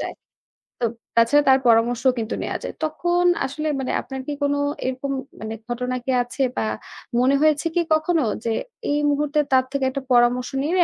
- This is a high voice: Yes, very high, 265 Hz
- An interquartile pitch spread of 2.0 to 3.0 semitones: No, average, 3.5 semitones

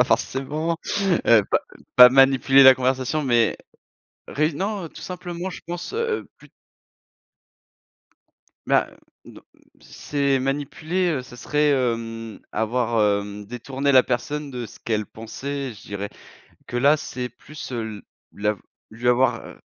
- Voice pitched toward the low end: Yes, low, 130 Hz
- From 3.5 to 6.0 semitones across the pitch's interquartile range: Yes, average, 4.2 semitones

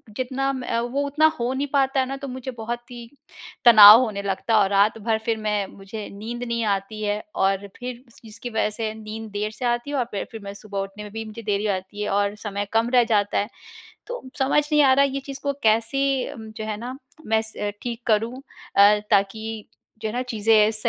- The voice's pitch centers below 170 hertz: No, high, 220 Hz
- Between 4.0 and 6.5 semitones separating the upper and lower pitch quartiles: No, average, 2.9 semitones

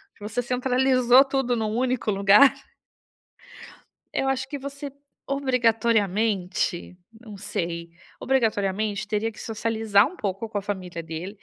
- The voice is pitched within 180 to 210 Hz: No, high, 220 Hz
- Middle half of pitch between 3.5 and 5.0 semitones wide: Yes, average, 4.1 semitones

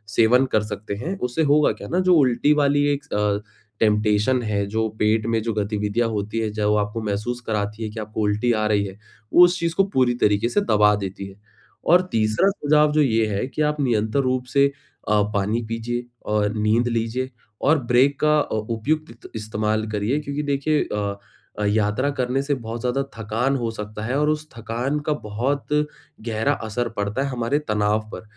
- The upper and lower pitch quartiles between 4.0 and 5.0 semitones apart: Yes, average, 4.6 semitones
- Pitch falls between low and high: No, low, 115 Hz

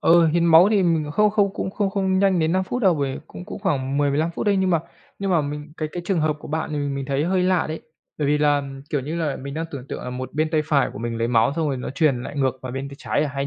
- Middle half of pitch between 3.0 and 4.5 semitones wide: Yes, average, 4.2 semitones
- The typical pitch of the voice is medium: Yes, medium, 155 Hz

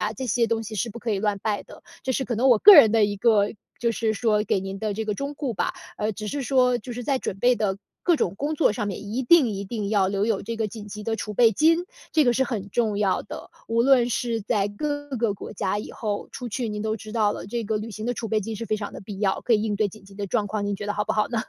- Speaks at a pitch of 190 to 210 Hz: No, high, 220 Hz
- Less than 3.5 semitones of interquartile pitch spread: Yes, average, 2.8 semitones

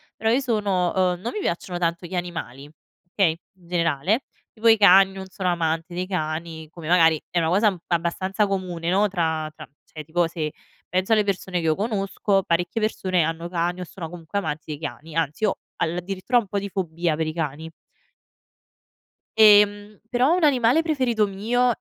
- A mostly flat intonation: No, average, 3.8 semitones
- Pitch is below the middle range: No, medium, 180 Hz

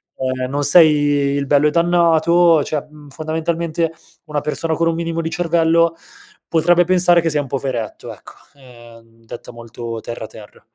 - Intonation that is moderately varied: Yes, average, 3.9 semitones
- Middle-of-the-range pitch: Yes, medium, 155 Hz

